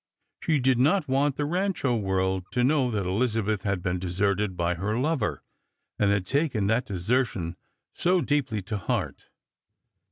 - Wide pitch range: Yes, wide, 6.1 semitones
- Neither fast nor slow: Yes, average, 155 wpm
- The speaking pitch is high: No, low, 110 Hz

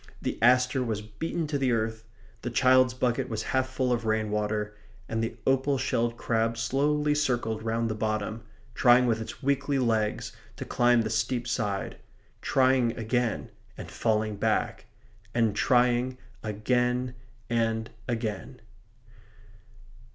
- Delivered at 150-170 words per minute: No, slow, 135 wpm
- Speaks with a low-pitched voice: Yes, low, 120 Hz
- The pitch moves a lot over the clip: No, narrow, 2.5 semitones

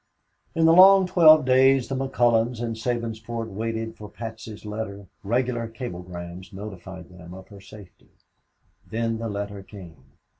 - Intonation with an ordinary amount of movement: Yes, average, 3.5 semitones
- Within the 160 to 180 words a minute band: No, average, 140 wpm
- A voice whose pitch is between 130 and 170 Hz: No, low, 110 Hz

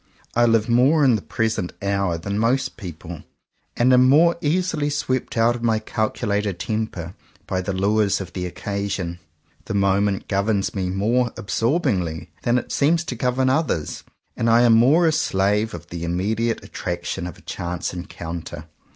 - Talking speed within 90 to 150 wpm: No, average, 170 wpm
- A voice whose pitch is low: Yes, low, 105 Hz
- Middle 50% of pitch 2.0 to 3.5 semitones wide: No, average, 4.9 semitones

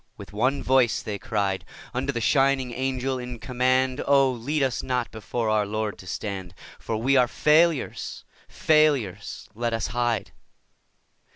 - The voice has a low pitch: Yes, low, 125 Hz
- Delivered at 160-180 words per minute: No, average, 150 wpm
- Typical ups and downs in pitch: Yes, average, 3.4 semitones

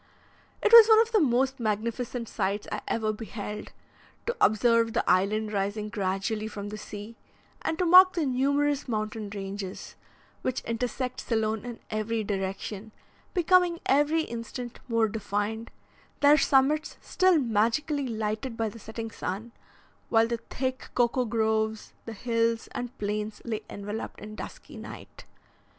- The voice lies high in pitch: Yes, high, 230 Hz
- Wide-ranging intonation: No, average, 3.4 semitones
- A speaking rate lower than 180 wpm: Yes, average, 140 wpm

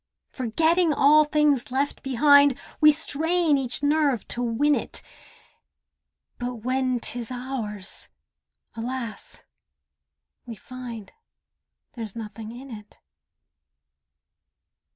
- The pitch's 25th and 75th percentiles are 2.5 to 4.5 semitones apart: Yes, average, 3.8 semitones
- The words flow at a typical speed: No, slow, 90 wpm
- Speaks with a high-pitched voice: Yes, very high, 255 Hz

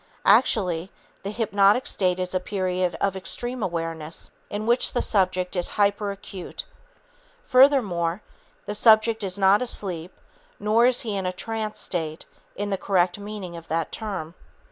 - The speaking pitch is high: Yes, high, 195 Hz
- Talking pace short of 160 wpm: Yes, average, 145 wpm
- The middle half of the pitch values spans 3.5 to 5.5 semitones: No, average, 3.0 semitones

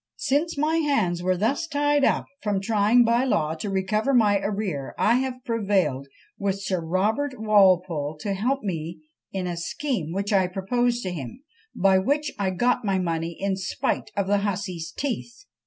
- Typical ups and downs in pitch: Yes, average, 4.9 semitones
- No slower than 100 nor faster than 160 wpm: No, average, 170 wpm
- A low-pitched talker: No, high, 200 Hz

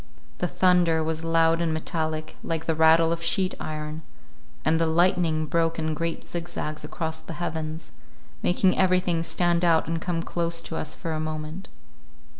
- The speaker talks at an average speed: Yes, average, 165 wpm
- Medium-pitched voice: Yes, medium, 165 Hz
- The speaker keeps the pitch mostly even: Yes, narrow, 1.3 semitones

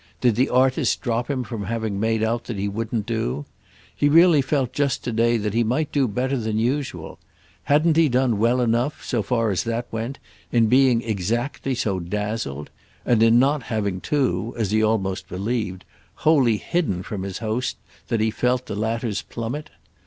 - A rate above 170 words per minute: Yes, average, 180 wpm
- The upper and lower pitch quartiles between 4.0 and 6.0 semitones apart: No, average, 3.1 semitones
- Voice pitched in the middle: No, low, 115 Hz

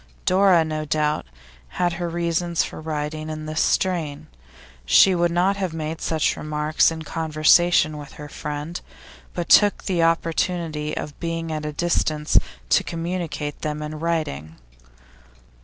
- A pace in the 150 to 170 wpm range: No, average, 140 wpm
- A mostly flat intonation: Yes, narrow, 2.2 semitones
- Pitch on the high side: No, medium, 160 Hz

